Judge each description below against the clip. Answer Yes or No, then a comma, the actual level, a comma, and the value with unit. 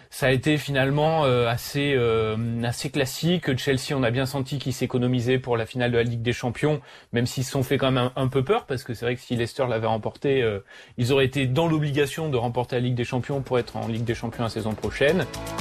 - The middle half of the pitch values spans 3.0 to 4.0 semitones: No, narrow, 2.6 semitones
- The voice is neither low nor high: No, low, 125 Hz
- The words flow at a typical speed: No, fast, 235 wpm